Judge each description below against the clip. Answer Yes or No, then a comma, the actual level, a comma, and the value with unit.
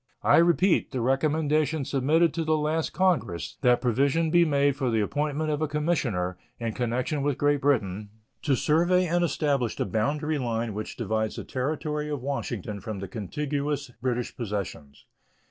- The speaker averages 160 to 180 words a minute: Yes, average, 165 wpm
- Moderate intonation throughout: Yes, average, 4.9 semitones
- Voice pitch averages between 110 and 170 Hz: Yes, medium, 140 Hz